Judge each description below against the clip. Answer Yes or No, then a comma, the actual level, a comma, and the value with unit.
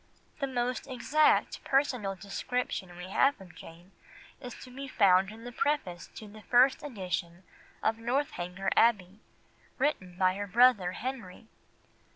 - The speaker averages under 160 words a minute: Yes, average, 145 wpm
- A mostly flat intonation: No, wide, 5.5 semitones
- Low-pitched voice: No, high, 220 Hz